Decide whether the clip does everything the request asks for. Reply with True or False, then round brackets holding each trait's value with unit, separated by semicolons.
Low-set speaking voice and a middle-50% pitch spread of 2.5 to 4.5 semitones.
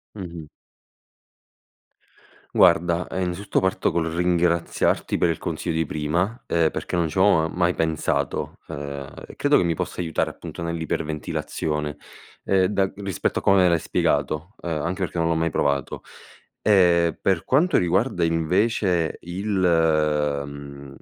True (85 Hz; 2.8 semitones)